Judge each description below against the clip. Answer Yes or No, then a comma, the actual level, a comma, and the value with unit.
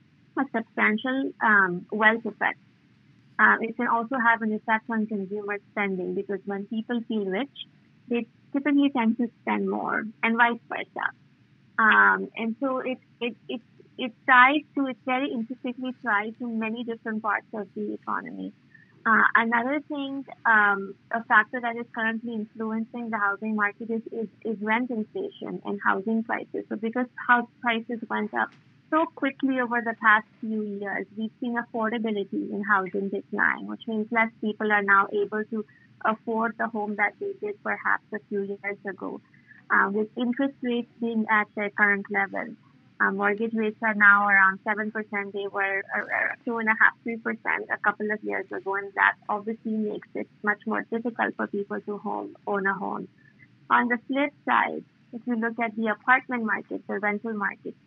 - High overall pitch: Yes, high, 220 Hz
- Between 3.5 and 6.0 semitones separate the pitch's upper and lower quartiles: No, average, 2.7 semitones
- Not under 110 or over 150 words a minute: No, average, 170 wpm